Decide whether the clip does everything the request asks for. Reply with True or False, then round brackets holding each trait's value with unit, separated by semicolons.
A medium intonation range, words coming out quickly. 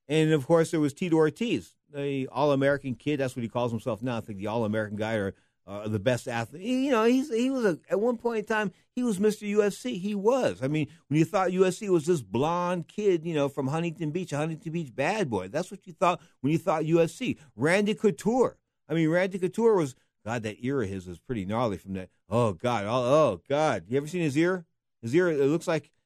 False (6.6 semitones; 235 wpm)